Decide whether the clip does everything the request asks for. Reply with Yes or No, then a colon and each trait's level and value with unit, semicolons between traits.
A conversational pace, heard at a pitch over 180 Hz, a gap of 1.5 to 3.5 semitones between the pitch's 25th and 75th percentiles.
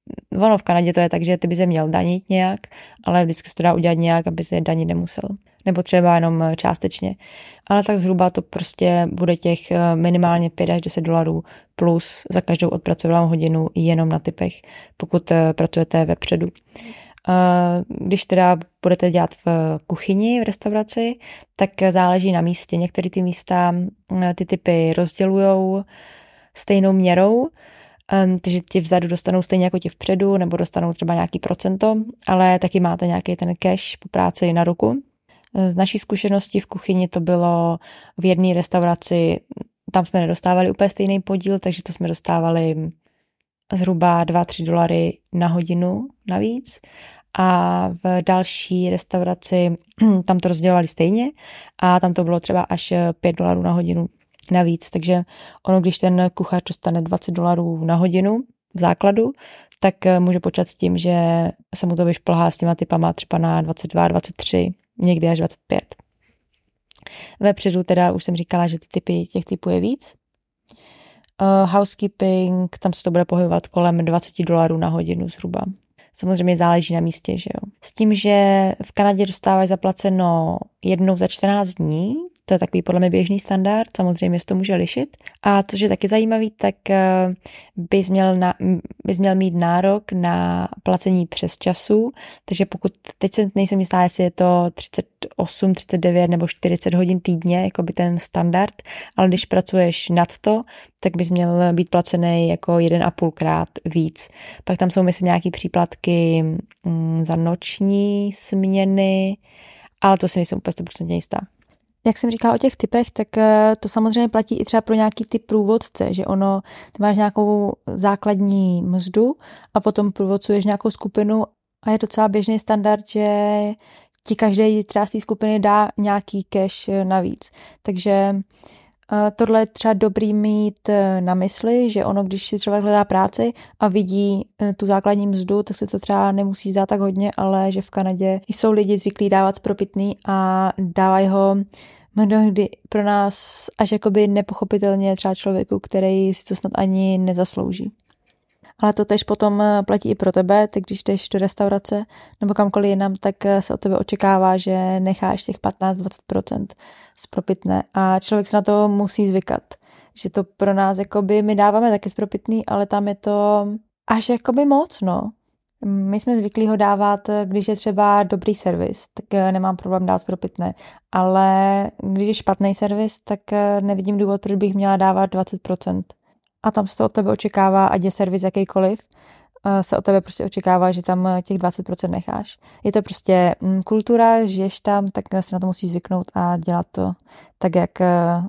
Yes: average, 160 wpm; high, 190 Hz; narrow, 2.6 semitones